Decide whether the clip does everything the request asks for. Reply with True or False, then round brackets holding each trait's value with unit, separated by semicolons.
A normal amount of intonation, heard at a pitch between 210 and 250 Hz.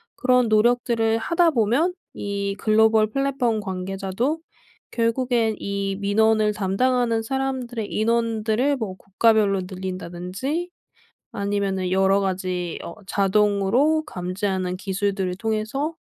True (3.7 semitones; 215 Hz)